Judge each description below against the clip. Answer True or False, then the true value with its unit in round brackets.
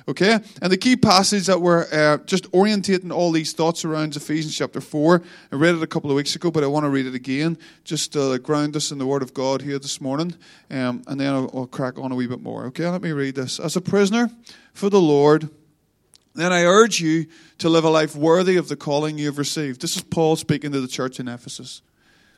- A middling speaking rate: False (240 wpm)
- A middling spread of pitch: True (4.0 semitones)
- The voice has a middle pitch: True (155 Hz)